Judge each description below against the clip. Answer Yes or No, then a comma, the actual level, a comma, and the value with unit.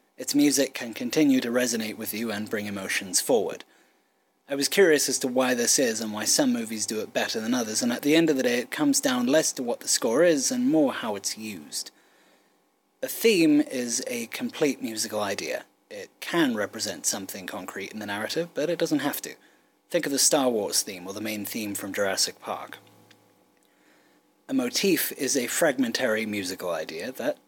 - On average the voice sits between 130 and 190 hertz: Yes, medium, 140 Hz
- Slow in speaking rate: No, average, 200 wpm